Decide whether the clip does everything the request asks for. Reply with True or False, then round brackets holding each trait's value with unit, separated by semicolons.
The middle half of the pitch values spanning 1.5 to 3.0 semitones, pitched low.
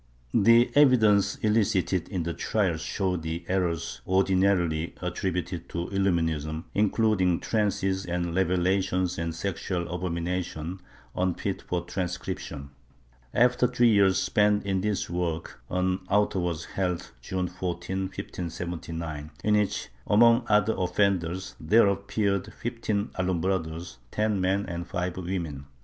True (2.7 semitones; 95 Hz)